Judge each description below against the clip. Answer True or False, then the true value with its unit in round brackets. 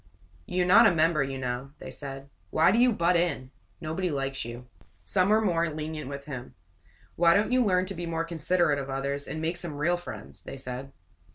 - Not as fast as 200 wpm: False (205 wpm)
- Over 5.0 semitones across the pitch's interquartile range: False (4.4 semitones)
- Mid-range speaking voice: True (160 Hz)